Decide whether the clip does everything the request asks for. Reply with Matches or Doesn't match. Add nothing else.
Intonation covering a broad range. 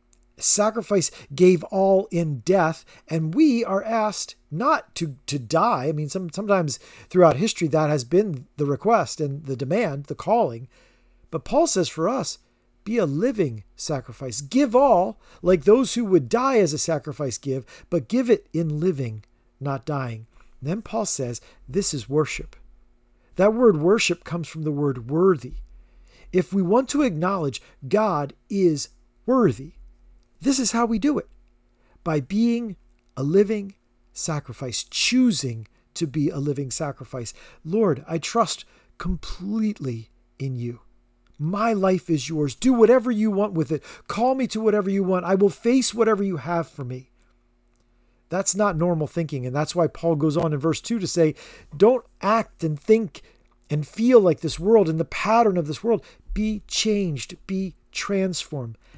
Matches